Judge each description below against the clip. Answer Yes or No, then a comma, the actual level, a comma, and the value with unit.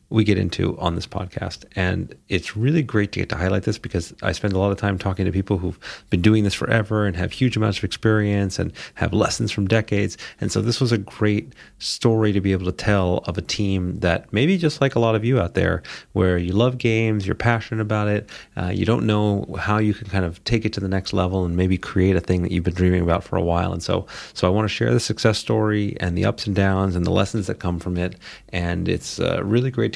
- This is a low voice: Yes, low, 100 Hz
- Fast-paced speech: Yes, fast, 260 wpm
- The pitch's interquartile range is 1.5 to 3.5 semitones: Yes, average, 3.1 semitones